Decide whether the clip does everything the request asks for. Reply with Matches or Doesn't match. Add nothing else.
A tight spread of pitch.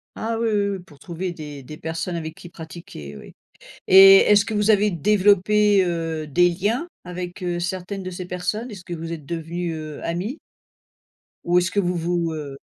Doesn't match